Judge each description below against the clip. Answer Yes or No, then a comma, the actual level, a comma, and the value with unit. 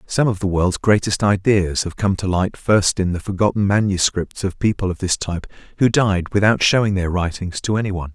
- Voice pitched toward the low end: Yes, very low, 95 Hz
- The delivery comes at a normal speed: No, fast, 215 wpm